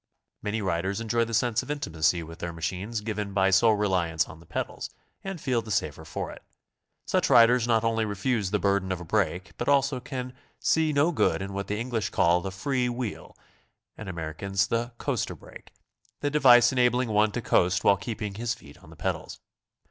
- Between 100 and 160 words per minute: No, average, 200 wpm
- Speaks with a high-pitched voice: No, low, 105 Hz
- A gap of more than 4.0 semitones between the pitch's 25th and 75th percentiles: Yes, average, 4.4 semitones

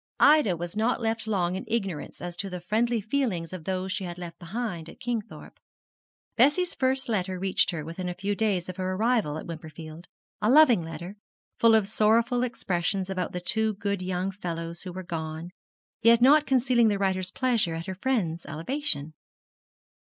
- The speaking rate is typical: Yes, average, 180 wpm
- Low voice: No, high, 190 Hz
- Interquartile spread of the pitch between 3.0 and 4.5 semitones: No, average, 4.9 semitones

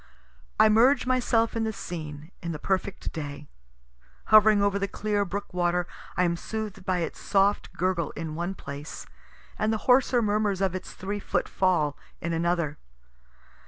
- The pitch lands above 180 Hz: Yes, high, 190 Hz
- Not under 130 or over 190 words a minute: Yes, average, 160 wpm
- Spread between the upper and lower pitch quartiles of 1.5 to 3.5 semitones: No, average, 4.0 semitones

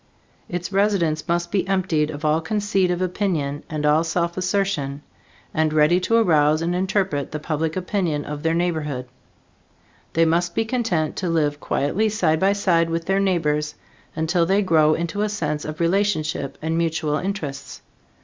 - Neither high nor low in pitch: Yes, medium, 165 Hz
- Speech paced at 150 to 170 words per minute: Yes, average, 165 wpm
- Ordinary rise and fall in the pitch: Yes, average, 3.6 semitones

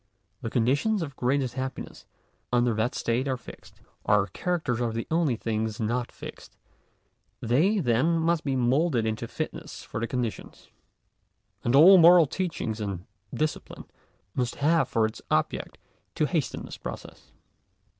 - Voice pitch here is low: Yes, low, 125 Hz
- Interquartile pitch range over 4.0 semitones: Yes, wide, 5.6 semitones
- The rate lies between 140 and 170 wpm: Yes, average, 145 wpm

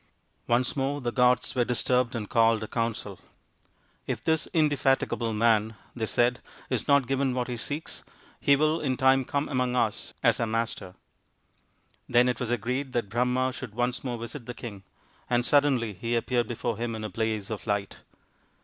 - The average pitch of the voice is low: Yes, low, 120 Hz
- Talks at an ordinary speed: Yes, average, 185 wpm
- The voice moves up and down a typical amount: No, narrow, 2.3 semitones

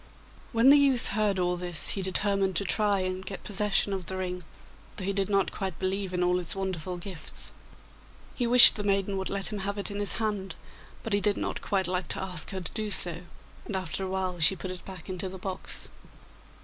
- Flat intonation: Yes, narrow, 1.8 semitones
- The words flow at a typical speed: No, fast, 225 wpm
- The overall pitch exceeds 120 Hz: Yes, high, 190 Hz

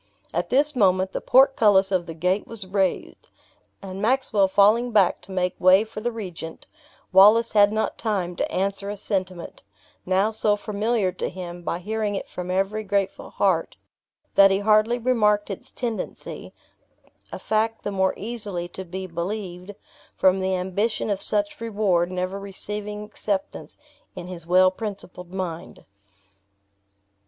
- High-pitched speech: Yes, high, 195 Hz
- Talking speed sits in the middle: Yes, average, 150 wpm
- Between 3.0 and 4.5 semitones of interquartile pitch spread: No, narrow, 2.5 semitones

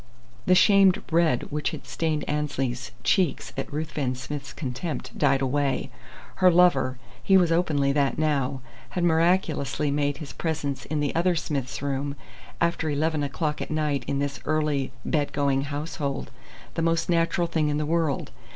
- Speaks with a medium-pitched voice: Yes, medium, 150 Hz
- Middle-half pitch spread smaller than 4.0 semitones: Yes, average, 2.9 semitones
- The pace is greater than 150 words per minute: Yes, average, 160 wpm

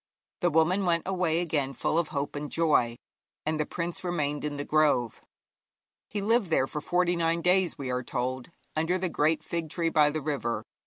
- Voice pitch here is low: No, medium, 160 Hz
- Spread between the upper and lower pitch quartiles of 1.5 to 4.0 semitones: Yes, average, 3.2 semitones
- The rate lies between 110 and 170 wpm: No, average, 195 wpm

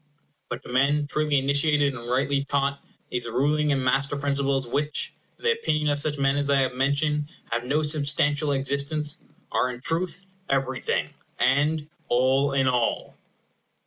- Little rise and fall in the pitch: Yes, narrow, 1.9 semitones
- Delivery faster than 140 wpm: Yes, average, 155 wpm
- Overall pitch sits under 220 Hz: Yes, medium, 140 Hz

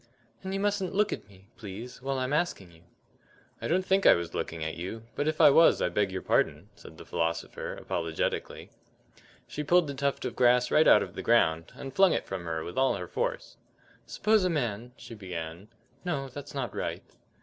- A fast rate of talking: Yes, fast, 210 wpm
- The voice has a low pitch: Yes, low, 125 Hz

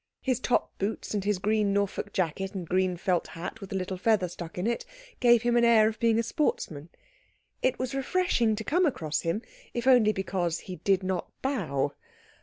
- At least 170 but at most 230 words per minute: Yes, average, 200 wpm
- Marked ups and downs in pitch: No, average, 4.5 semitones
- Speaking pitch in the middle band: No, high, 200 Hz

